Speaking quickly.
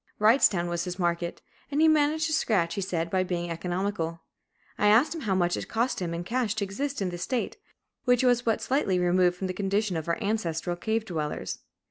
Yes: fast, 210 wpm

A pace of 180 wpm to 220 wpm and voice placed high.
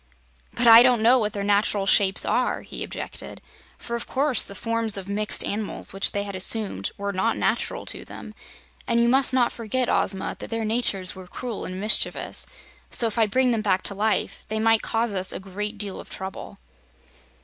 Yes: average, 200 wpm; high, 215 Hz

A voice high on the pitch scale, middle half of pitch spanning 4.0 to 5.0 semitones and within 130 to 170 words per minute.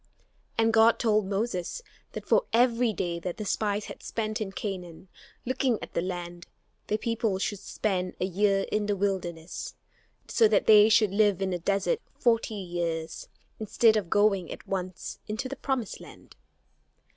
No: high, 205 Hz; average, 3.3 semitones; average, 165 wpm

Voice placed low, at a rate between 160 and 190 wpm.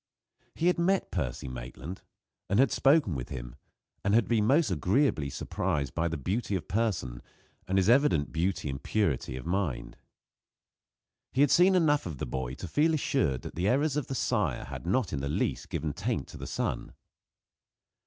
Yes: very low, 95 Hz; average, 185 wpm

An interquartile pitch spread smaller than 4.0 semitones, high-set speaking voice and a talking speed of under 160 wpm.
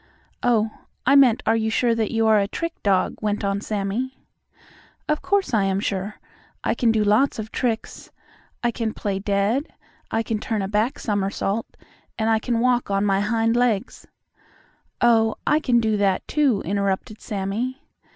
No: average, 3.0 semitones; high, 220 Hz; average, 175 wpm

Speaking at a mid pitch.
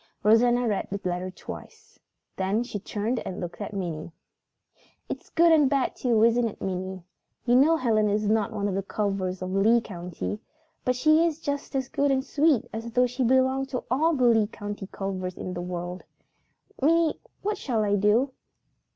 No: high, 225 Hz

